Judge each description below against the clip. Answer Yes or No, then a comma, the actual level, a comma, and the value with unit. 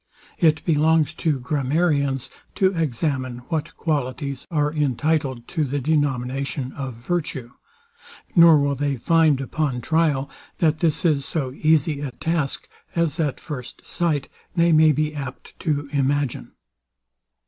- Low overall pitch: No, medium, 145 Hz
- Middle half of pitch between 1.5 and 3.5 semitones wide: Yes, average, 2.9 semitones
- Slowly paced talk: Yes, slow, 130 wpm